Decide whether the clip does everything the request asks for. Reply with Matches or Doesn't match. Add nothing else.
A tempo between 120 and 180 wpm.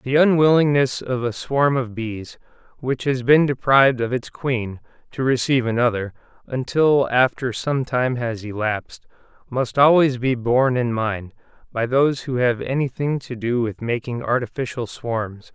Matches